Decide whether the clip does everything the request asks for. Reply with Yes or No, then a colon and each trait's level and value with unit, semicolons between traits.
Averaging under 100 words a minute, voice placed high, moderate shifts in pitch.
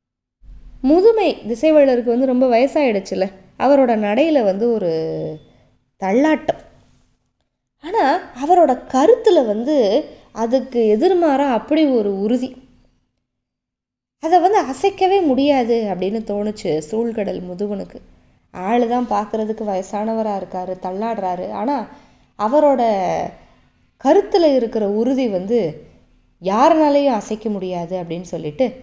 No: average, 90 wpm; high, 235 Hz; wide, 6.1 semitones